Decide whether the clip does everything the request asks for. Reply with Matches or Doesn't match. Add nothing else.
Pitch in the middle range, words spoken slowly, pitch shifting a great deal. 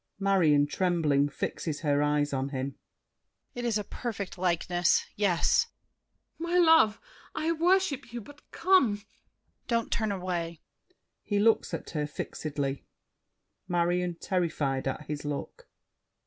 Matches